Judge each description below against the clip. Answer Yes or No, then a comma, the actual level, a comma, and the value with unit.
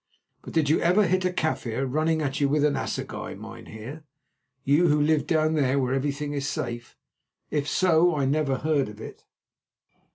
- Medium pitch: Yes, medium, 150 Hz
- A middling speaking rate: Yes, average, 175 wpm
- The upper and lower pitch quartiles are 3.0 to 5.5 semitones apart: No, narrow, 2.6 semitones